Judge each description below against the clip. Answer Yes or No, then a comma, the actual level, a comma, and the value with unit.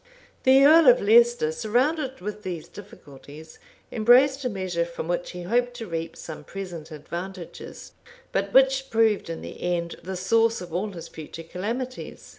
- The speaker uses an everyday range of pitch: No, wide, 6.2 semitones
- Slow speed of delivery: No, average, 160 wpm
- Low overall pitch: No, high, 195 Hz